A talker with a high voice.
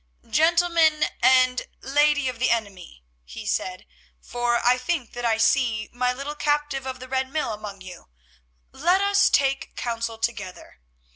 Yes: very high, 255 Hz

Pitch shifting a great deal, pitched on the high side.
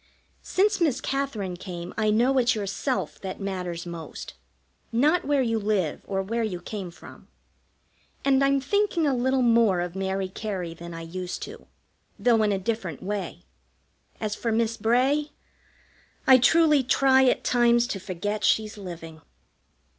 Yes: wide, 5.7 semitones; high, 220 Hz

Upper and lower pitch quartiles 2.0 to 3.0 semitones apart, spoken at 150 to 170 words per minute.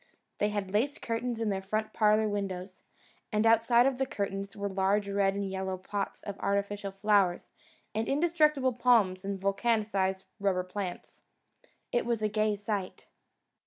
Yes: narrow, 2.6 semitones; average, 155 wpm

